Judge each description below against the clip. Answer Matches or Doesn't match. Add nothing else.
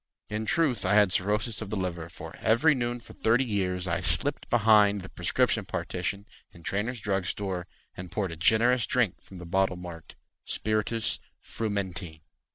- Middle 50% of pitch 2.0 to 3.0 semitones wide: Doesn't match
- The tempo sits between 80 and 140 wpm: Doesn't match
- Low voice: Matches